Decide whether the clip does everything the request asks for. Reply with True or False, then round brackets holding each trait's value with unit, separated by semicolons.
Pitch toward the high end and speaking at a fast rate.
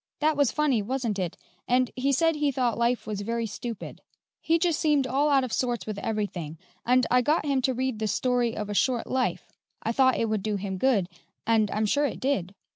True (245 Hz; 220 wpm)